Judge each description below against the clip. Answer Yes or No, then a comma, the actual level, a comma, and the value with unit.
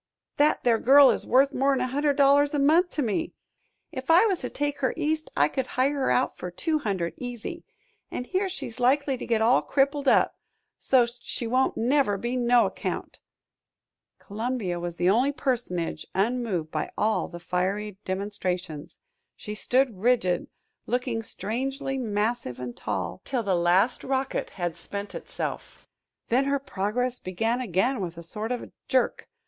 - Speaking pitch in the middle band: No, high, 245 Hz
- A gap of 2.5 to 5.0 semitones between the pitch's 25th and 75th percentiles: No, wide, 5.4 semitones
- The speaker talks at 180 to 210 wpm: No, average, 165 wpm